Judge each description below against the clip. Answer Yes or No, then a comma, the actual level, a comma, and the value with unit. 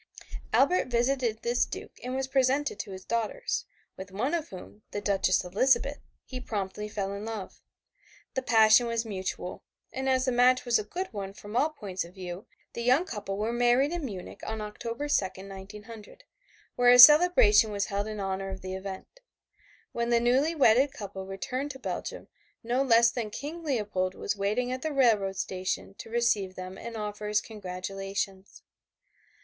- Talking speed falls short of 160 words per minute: No, average, 175 wpm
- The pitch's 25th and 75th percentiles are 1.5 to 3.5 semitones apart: No, average, 4.5 semitones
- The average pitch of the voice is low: No, high, 220 Hz